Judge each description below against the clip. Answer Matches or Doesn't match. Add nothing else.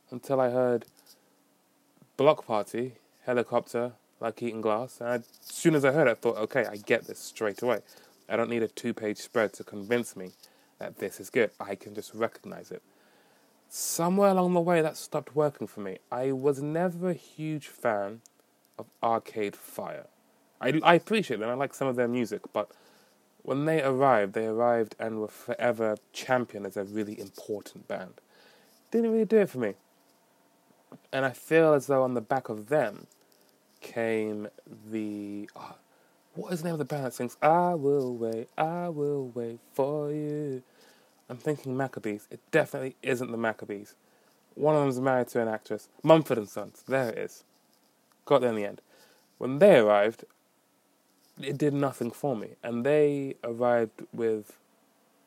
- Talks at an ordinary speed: Matches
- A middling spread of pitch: Matches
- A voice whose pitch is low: Matches